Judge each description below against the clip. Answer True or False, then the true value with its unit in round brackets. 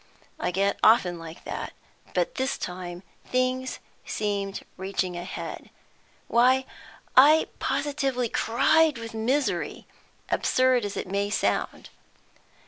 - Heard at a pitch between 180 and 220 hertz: False (230 Hz)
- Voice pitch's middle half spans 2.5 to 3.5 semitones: False (4.9 semitones)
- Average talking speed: False (115 wpm)